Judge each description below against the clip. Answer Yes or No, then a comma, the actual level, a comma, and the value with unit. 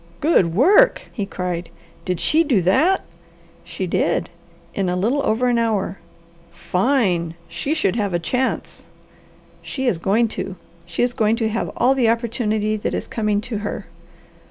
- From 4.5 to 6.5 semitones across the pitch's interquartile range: Yes, average, 5.1 semitones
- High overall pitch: Yes, high, 215 Hz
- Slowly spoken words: No, average, 160 wpm